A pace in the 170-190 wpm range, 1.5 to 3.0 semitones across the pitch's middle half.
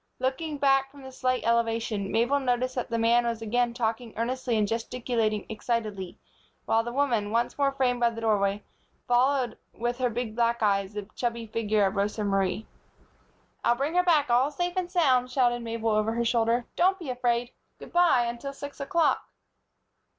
Yes: average, 180 wpm; average, 2.7 semitones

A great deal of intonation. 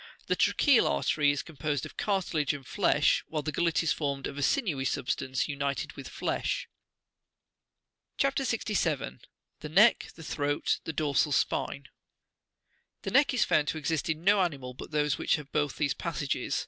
No: average, 2.9 semitones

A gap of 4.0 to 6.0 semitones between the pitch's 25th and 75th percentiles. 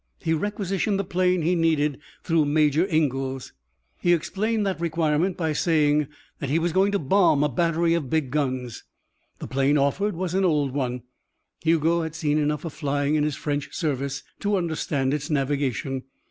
No: average, 3.3 semitones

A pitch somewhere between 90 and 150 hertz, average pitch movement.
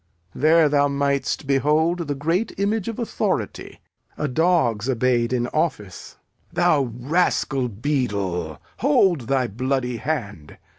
Yes: medium, 140 Hz; average, 5.0 semitones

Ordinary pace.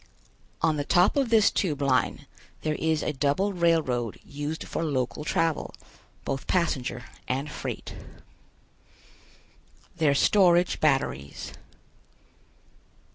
No: slow, 105 wpm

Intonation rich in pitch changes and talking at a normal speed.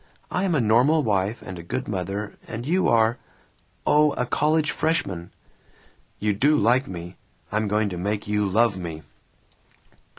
Yes: wide, 5.7 semitones; average, 160 wpm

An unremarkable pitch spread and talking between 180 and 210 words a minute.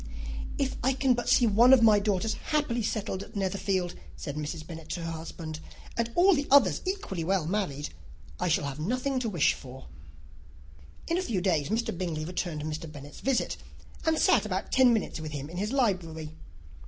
No: wide, 7.2 semitones; average, 190 wpm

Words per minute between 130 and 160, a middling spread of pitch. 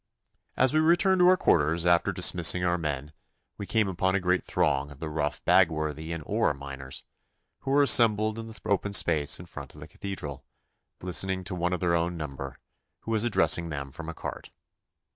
No: average, 195 wpm; average, 4.9 semitones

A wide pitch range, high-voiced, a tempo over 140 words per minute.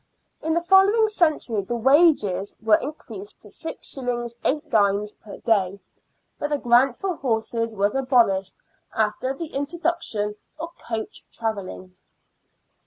No: wide, 6.5 semitones; high, 240 Hz; slow, 135 wpm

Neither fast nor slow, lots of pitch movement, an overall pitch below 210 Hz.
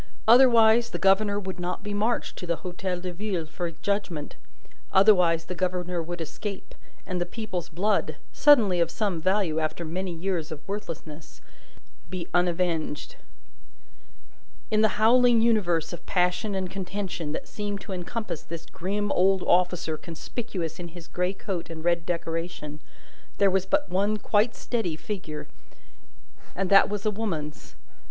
No: average, 150 wpm; average, 3.4 semitones; medium, 185 Hz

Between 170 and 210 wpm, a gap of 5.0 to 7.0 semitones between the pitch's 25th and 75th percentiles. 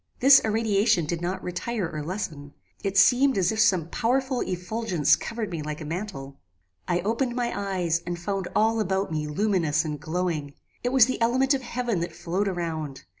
Yes: average, 180 wpm; wide, 5.5 semitones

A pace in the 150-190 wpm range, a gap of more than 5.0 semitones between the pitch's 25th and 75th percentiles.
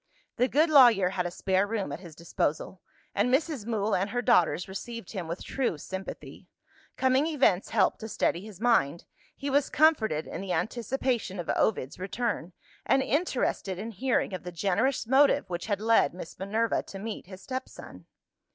Yes: average, 175 wpm; wide, 5.6 semitones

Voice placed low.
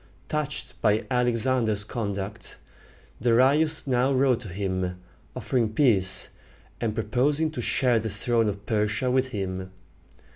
Yes: low, 115 Hz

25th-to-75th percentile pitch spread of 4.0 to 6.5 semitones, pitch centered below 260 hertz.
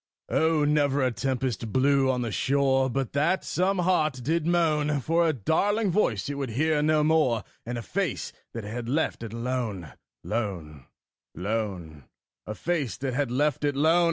Yes: average, 5.0 semitones; low, 135 Hz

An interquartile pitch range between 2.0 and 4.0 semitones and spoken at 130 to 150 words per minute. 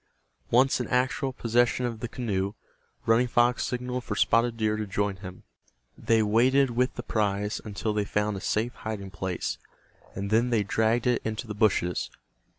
No: average, 2.9 semitones; average, 170 wpm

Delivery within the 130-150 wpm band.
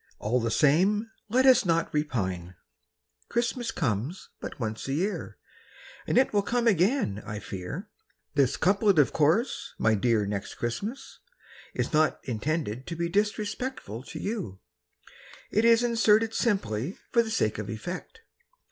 Yes: average, 145 wpm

